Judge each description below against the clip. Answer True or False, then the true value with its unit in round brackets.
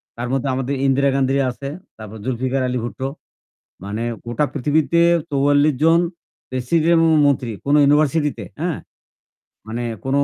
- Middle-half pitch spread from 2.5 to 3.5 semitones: True (2.8 semitones)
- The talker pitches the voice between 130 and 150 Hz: True (135 Hz)